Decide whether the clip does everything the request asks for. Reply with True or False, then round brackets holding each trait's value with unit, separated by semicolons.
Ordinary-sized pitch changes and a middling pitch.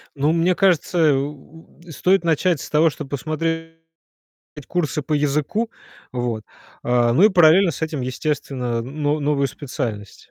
True (3.5 semitones; 150 Hz)